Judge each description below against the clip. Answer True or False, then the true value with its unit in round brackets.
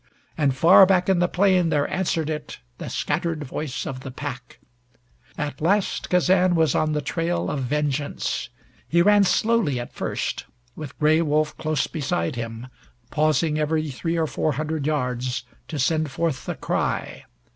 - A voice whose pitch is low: False (155 Hz)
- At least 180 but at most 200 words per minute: False (160 wpm)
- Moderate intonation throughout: True (3.2 semitones)